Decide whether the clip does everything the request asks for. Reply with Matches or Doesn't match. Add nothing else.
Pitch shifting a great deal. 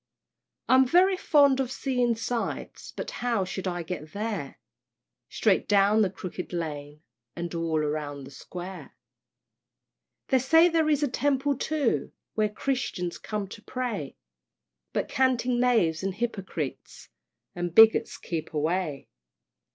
Matches